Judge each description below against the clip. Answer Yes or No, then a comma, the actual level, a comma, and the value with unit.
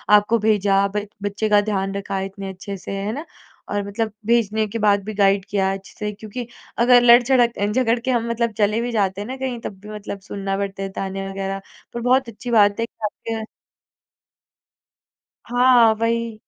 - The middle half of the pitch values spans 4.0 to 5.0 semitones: No, average, 2.8 semitones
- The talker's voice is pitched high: Yes, high, 210 Hz